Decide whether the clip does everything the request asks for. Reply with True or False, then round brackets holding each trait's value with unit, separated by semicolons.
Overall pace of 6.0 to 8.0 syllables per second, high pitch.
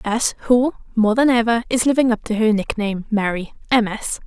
False (5.4 syllables/s; 225 Hz)